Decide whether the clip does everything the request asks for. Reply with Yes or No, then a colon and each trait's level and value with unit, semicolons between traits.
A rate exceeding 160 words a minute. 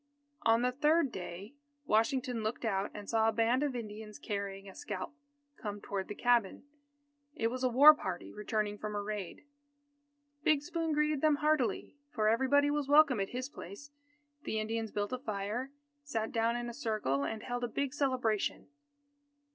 Yes: average, 170 wpm